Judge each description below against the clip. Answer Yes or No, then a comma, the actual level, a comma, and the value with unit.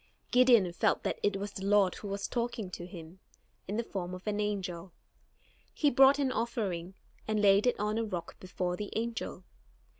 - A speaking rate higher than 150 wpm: Yes, average, 185 wpm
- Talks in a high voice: Yes, high, 205 Hz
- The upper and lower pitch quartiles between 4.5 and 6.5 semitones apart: No, average, 3.8 semitones